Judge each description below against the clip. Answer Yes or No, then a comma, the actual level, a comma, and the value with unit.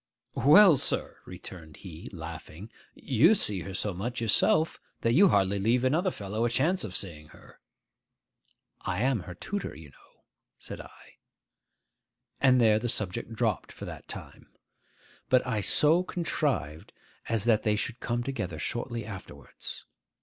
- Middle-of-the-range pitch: No, low, 110 Hz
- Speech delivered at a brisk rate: No, average, 150 wpm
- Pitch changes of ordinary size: No, wide, 5.7 semitones